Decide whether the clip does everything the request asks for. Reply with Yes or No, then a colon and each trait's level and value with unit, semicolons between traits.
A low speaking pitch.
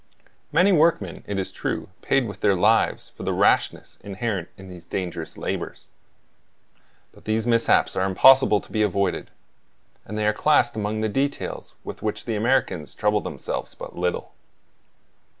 Yes: low, 105 Hz